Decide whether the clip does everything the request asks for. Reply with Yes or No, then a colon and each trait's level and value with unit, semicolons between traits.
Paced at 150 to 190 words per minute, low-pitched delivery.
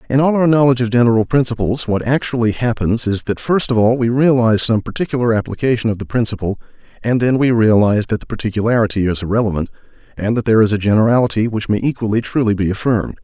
No: average, 200 wpm; low, 115 Hz